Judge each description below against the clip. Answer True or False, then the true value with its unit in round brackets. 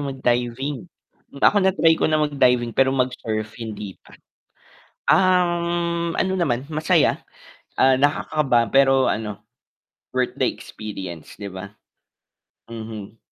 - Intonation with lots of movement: True (5.8 semitones)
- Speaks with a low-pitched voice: True (130 Hz)